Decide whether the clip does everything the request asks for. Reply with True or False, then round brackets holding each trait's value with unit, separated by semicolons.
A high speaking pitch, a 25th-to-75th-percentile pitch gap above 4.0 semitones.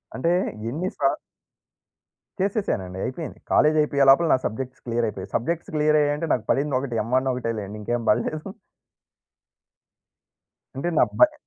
False (135 Hz; 4.6 semitones)